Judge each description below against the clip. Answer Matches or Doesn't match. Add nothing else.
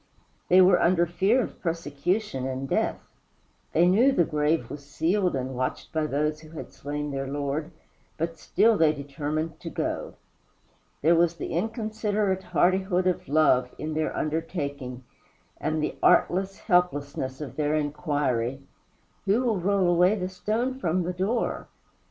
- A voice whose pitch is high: Doesn't match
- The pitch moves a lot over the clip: Doesn't match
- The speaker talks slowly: Doesn't match